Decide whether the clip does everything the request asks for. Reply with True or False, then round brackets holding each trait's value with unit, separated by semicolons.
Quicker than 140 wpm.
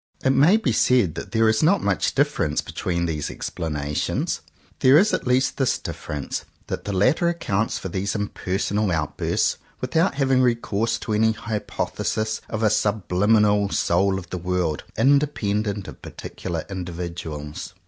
True (155 wpm)